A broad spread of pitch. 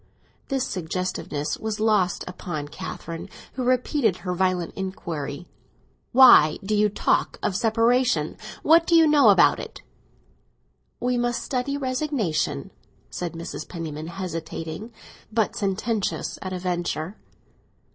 Yes: wide, 6.2 semitones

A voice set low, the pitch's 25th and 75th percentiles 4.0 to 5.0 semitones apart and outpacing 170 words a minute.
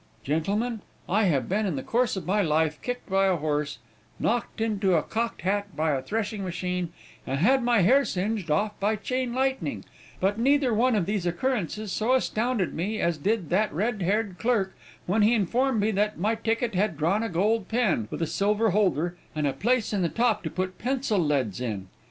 No: high, 205 Hz; average, 4.6 semitones; average, 200 wpm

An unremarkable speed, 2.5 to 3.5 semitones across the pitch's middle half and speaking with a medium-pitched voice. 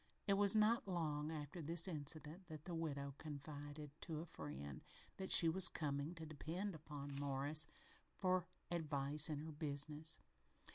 Yes: average, 150 wpm; average, 2.9 semitones; medium, 155 Hz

